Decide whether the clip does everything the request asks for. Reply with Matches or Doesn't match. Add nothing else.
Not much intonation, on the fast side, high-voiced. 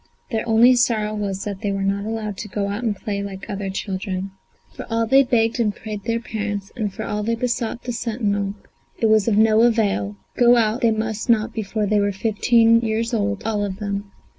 Matches